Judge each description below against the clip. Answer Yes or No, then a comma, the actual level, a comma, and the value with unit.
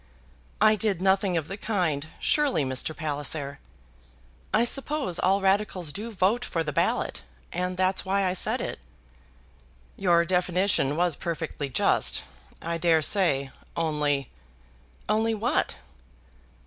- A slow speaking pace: Yes, slow, 130 wpm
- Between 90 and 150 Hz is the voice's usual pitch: No, medium, 180 Hz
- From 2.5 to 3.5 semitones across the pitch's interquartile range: No, average, 4.5 semitones